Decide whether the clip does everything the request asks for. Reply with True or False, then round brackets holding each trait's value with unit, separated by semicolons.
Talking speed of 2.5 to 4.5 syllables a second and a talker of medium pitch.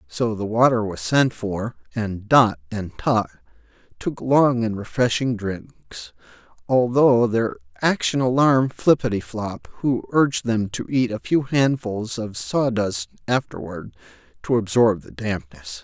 False (4.0 syllables/s; 110 Hz)